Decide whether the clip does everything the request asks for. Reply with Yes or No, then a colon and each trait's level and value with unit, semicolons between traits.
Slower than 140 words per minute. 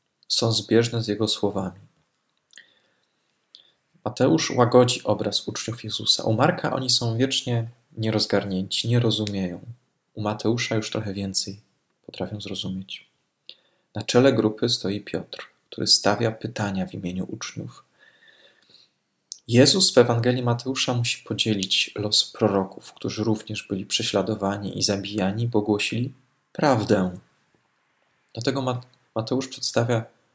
Yes: slow, 110 wpm